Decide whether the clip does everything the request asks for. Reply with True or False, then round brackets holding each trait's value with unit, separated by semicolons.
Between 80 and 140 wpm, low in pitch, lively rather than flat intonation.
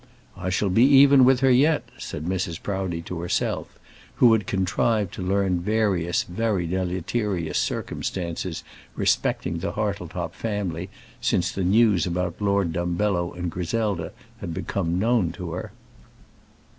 False (135 wpm; 95 Hz; 3.3 semitones)